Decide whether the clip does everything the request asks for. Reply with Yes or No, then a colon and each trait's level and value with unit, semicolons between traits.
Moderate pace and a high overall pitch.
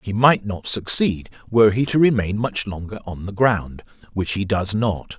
No: average, 185 wpm; low, 105 Hz